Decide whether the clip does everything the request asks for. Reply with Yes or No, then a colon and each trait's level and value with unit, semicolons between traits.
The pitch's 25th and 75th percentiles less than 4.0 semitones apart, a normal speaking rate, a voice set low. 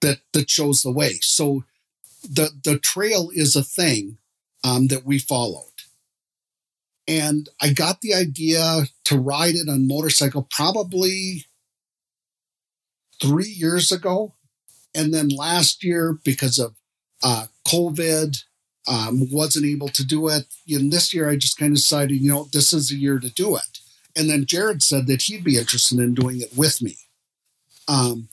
No: average, 3.1 semitones; average, 160 wpm; medium, 145 Hz